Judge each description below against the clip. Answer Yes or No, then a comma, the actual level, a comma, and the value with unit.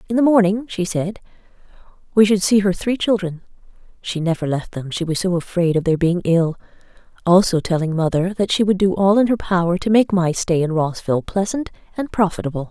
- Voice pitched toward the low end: No, medium, 185 Hz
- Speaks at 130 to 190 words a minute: No, fast, 205 wpm